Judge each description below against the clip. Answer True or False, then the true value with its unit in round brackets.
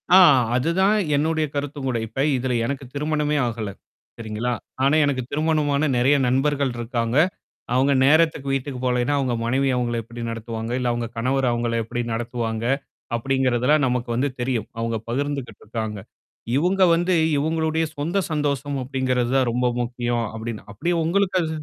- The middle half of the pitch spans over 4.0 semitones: False (3.6 semitones)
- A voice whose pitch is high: False (130 Hz)